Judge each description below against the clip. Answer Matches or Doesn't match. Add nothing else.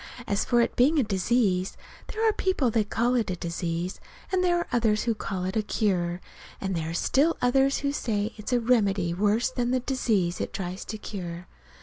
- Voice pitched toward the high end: Matches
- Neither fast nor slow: Doesn't match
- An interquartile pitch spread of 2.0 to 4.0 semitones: Doesn't match